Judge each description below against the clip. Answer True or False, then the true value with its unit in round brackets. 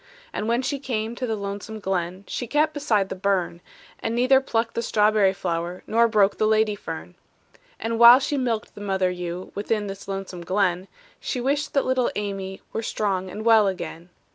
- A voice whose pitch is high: True (210 Hz)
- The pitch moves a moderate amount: True (3.5 semitones)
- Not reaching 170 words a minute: False (190 wpm)